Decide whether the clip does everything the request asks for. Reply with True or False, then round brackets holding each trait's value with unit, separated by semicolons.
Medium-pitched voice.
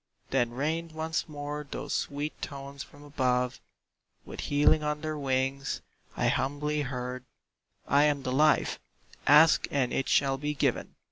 True (145 Hz)